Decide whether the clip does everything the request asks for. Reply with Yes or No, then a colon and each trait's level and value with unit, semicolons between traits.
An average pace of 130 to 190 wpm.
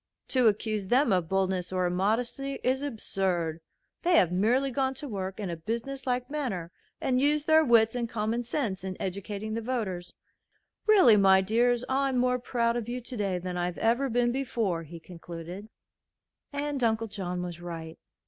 Yes: average, 170 wpm